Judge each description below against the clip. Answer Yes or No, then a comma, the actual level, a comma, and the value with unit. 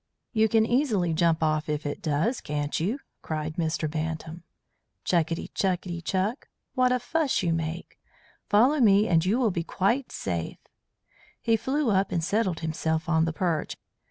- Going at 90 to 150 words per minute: No, average, 160 wpm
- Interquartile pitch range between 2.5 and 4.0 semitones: No, wide, 5.6 semitones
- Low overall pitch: No, medium, 175 Hz